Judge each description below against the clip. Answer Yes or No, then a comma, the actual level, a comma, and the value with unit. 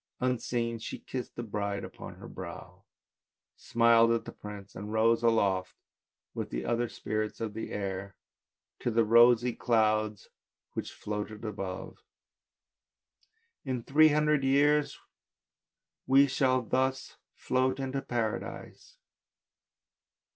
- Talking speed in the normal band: No, slow, 120 wpm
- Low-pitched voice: Yes, low, 115 Hz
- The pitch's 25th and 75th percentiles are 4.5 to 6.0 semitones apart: No, average, 3.2 semitones